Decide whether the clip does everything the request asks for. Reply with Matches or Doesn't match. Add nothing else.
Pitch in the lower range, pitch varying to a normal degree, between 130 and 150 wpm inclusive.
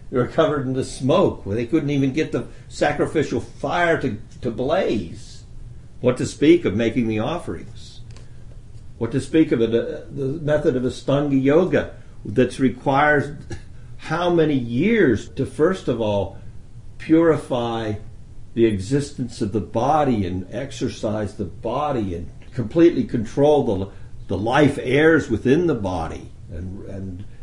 Matches